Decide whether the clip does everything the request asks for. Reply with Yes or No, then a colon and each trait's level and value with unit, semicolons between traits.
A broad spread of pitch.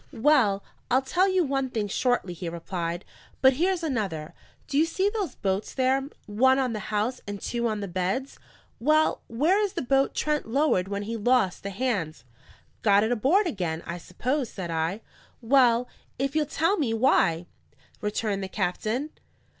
Yes: wide, 5.8 semitones